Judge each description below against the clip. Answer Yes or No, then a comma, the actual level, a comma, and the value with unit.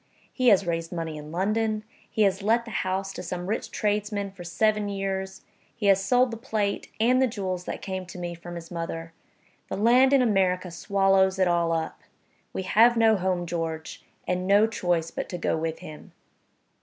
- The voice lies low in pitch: No, high, 190 Hz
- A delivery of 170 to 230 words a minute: Yes, average, 195 wpm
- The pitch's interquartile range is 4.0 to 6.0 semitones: No, average, 3.5 semitones